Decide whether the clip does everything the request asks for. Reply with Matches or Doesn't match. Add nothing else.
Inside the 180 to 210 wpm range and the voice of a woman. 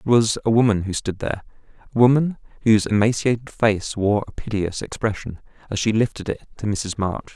Doesn't match